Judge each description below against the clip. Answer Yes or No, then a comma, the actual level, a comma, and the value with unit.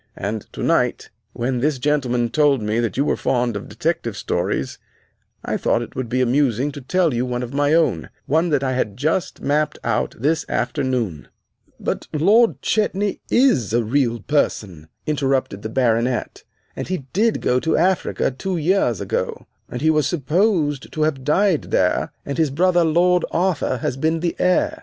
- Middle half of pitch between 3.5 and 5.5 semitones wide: Yes, average, 5.1 semitones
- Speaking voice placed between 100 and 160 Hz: Yes, medium, 140 Hz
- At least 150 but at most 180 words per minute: Yes, average, 170 wpm